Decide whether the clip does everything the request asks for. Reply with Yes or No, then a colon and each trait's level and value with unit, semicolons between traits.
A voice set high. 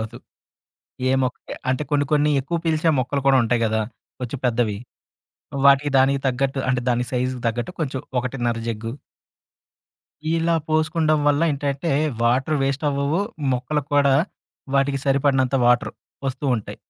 No: low, 135 Hz